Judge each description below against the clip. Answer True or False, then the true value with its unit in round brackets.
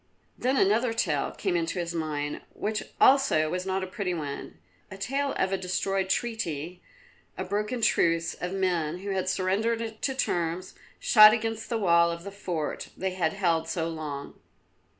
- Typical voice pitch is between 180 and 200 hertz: True (185 Hz)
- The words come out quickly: False (170 wpm)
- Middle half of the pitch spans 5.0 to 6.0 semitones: False (4.1 semitones)